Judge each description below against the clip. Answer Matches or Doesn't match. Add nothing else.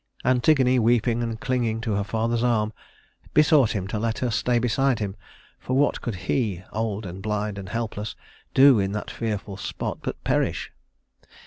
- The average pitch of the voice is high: Doesn't match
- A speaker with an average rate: Matches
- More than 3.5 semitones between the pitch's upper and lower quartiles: Doesn't match